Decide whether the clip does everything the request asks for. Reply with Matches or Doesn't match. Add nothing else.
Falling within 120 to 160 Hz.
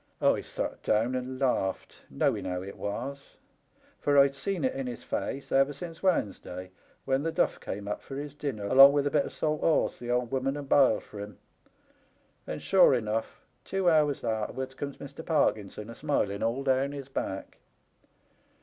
Matches